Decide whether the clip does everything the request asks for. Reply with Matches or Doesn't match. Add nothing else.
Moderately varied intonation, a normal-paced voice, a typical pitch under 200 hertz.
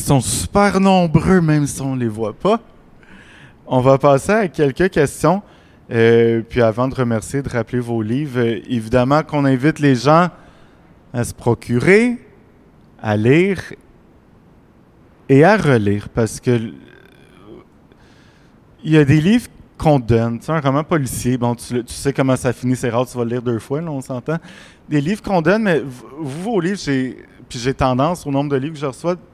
Matches